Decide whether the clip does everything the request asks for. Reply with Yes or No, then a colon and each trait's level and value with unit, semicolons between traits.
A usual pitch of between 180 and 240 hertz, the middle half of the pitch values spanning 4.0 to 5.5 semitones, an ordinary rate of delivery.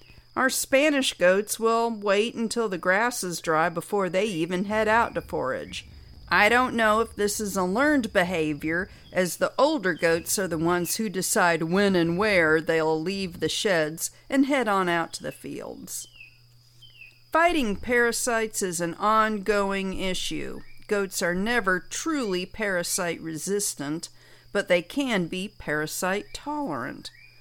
Yes: high, 190 Hz; average, 4.8 semitones; average, 145 wpm